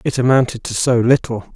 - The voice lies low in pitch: Yes, low, 125 Hz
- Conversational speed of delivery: Yes, average, 195 wpm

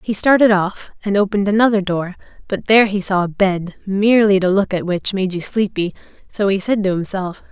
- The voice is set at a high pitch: Yes, high, 195 Hz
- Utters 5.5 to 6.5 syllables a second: Yes, 5.6 syllables/s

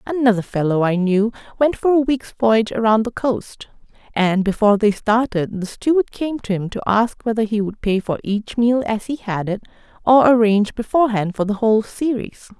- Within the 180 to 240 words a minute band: Yes, average, 195 wpm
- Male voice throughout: No, female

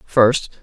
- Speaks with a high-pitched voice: No, low, 120 Hz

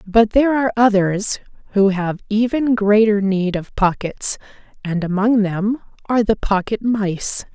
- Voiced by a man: No, female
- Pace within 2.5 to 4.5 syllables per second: Yes, 4.4 syllables/s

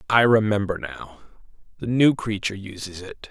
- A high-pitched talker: No, low, 105 Hz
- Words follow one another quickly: No, average, 145 wpm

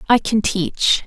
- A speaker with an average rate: Yes, average, 170 wpm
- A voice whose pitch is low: No, high, 210 Hz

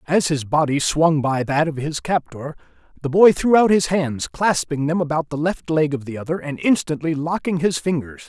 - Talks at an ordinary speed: No, fast, 210 wpm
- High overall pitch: No, medium, 150 Hz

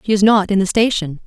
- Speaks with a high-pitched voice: Yes, high, 200 Hz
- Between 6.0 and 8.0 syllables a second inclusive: Yes, 6.4 syllables/s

